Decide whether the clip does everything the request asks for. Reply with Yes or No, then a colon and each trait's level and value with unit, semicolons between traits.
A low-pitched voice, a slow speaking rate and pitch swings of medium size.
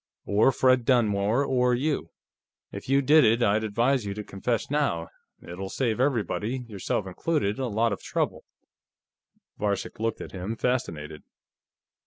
No: low, 115 Hz; average, 145 wpm; average, 4.2 semitones